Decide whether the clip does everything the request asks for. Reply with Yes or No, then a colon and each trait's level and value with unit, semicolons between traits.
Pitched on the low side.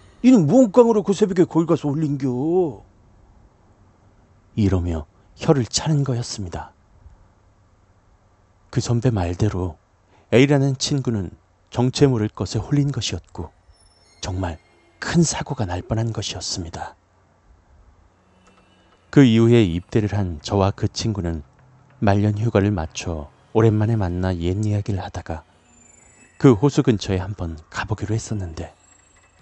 Yes: low, 100 Hz